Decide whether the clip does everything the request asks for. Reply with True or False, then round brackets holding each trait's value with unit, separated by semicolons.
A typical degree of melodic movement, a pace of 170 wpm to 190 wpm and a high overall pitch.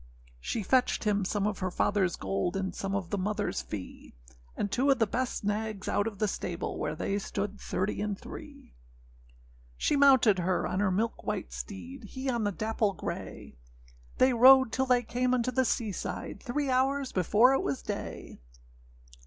True (4.8 semitones; 185 wpm; 210 Hz)